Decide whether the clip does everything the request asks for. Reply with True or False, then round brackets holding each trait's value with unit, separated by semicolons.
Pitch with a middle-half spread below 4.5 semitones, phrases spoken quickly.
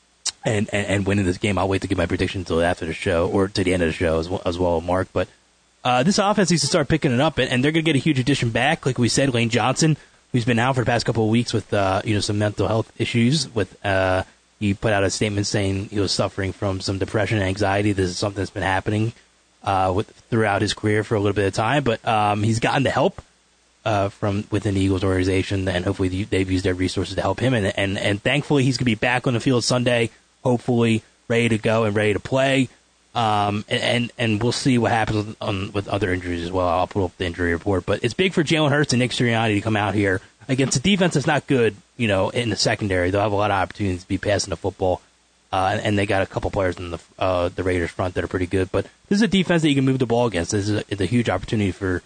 True (4.1 semitones; 275 wpm)